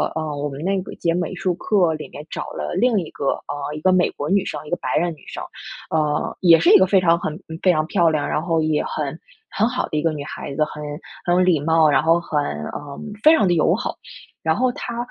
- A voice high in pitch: No, medium, 165 Hz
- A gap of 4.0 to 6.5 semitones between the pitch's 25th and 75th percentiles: No, average, 3.4 semitones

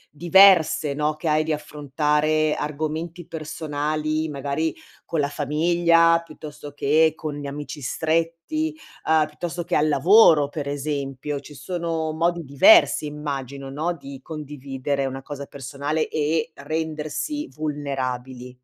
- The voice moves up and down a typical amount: No, narrow, 2.2 semitones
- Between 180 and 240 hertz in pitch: No, medium, 150 Hz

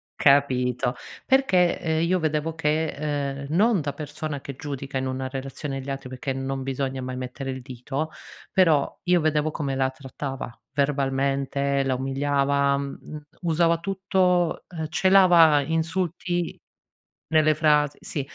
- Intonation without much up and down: No, average, 3.0 semitones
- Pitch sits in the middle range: Yes, medium, 145 Hz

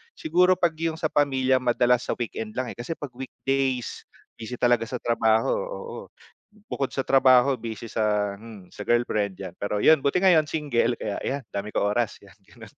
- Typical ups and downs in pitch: Yes, average, 4.1 semitones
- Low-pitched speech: Yes, low, 125 Hz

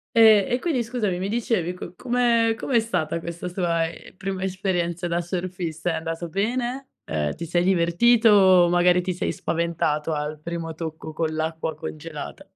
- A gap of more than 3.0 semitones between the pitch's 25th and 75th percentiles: Yes, average, 4.0 semitones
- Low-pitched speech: No, medium, 175 Hz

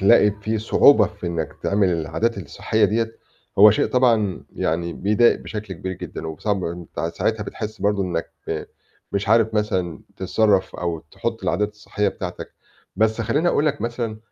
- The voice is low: Yes, low, 105 Hz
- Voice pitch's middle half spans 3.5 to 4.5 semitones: No, average, 3.1 semitones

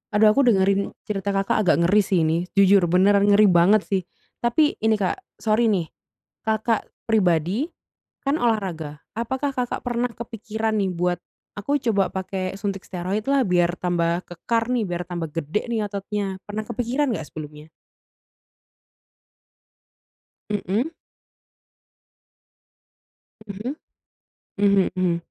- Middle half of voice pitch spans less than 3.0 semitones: No, average, 3.6 semitones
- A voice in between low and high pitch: No, high, 200 Hz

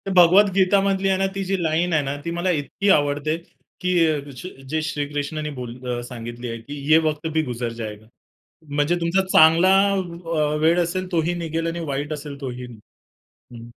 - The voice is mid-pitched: Yes, medium, 155 Hz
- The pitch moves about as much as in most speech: Yes, average, 3.6 semitones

